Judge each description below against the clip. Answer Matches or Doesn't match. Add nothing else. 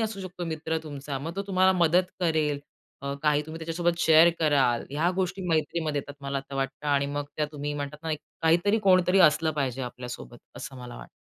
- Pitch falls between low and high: Matches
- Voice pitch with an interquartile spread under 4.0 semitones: Matches